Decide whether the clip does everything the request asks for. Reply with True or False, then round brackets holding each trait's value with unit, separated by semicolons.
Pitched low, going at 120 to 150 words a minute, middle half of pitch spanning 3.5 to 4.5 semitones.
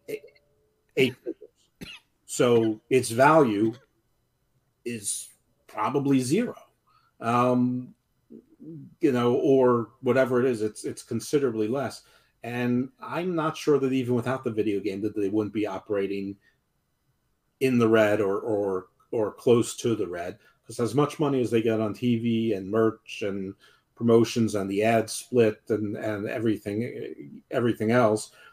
False (115 Hz; 135 wpm; 3.0 semitones)